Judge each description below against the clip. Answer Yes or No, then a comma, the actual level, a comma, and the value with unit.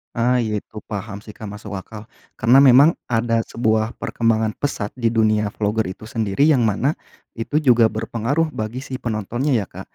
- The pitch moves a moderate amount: No, narrow, 2.3 semitones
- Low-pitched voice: Yes, low, 115 Hz